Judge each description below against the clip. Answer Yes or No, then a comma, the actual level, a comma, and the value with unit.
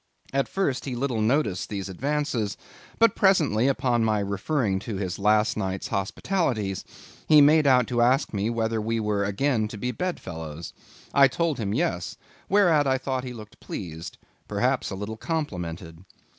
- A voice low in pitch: Yes, low, 115 Hz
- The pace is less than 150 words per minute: No, average, 160 wpm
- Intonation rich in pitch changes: Yes, wide, 5.7 semitones